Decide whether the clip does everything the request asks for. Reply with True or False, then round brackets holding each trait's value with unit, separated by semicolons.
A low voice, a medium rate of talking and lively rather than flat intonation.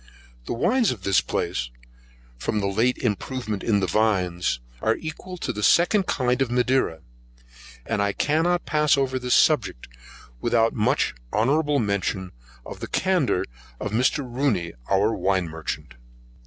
True (115 Hz; 145 wpm; 6.0 semitones)